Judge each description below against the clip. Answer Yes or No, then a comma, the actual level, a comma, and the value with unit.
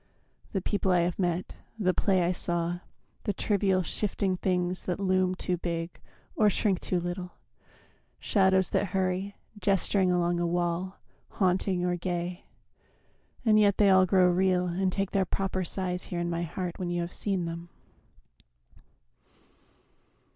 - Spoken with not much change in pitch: Yes, narrow, 1.6 semitones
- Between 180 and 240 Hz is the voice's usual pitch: Yes, medium, 185 Hz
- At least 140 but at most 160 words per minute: Yes, average, 150 wpm